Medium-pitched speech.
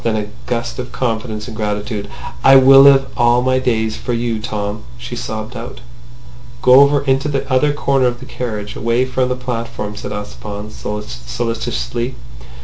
No: low, 120 Hz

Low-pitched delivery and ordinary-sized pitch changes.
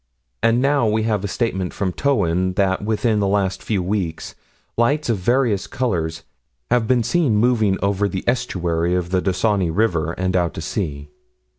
Yes: low, 100 Hz; average, 4.2 semitones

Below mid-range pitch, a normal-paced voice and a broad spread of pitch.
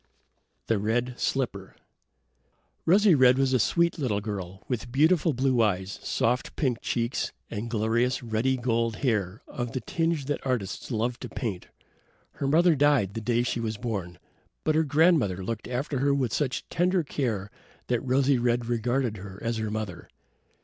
No: low, 120 Hz; average, 165 wpm; average, 3.8 semitones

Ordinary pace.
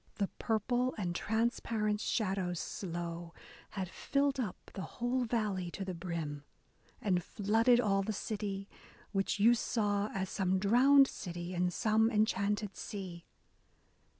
No: slow, 130 wpm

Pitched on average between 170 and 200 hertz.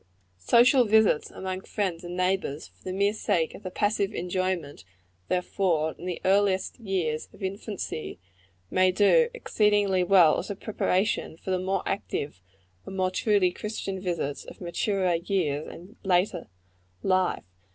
Yes: medium, 185 Hz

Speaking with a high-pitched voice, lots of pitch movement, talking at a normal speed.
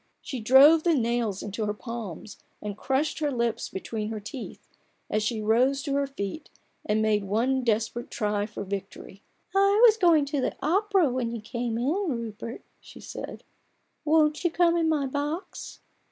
Yes: high, 245 Hz; wide, 5.8 semitones; average, 180 wpm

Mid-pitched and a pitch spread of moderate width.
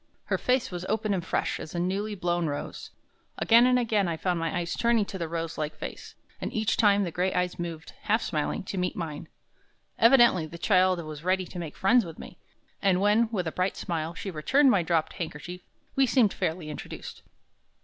Yes: medium, 180 Hz; average, 4.2 semitones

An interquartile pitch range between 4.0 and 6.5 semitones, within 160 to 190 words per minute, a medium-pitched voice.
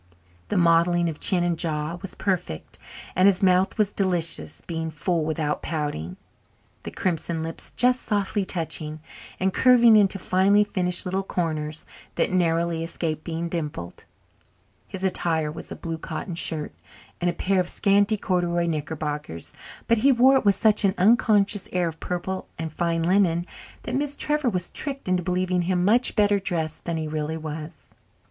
No: average, 3.4 semitones; average, 165 wpm; medium, 175 Hz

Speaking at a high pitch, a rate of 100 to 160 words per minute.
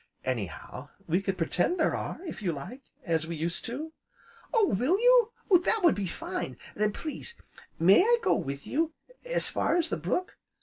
No: high, 245 Hz; average, 185 wpm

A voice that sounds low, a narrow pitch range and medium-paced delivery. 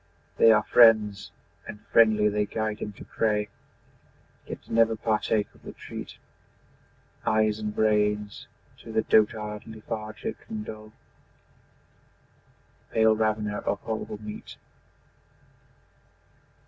No: low, 110 Hz; narrow, 0.9 semitones; slow, 110 wpm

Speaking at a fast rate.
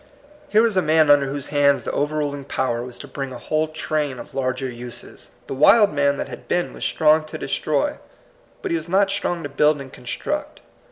Yes: fast, 215 wpm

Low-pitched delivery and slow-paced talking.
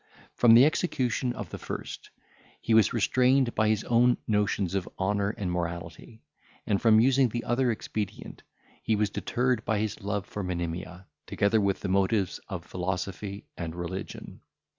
No: low, 105 Hz; average, 160 wpm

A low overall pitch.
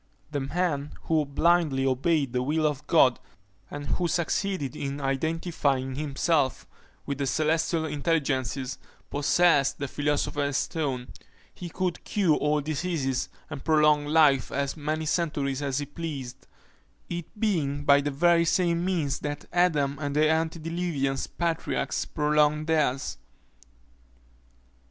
No: medium, 150 Hz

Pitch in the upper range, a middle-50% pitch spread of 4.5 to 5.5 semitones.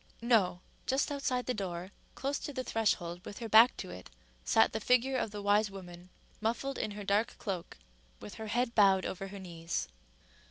Yes: high, 205 Hz; average, 4.8 semitones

